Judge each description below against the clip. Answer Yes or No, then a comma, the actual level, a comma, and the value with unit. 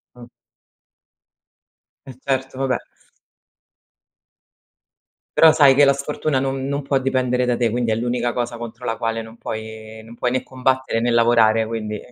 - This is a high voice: No, low, 120 Hz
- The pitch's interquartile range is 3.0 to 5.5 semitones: No, narrow, 2.6 semitones